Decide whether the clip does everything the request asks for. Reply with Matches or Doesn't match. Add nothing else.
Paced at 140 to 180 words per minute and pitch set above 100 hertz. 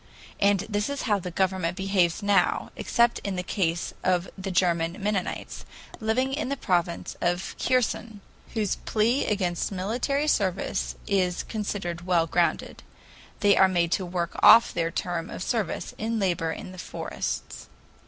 Matches